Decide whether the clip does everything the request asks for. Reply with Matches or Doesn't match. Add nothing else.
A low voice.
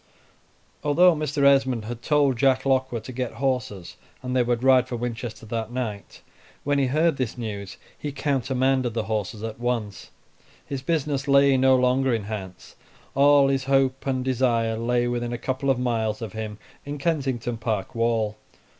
Matches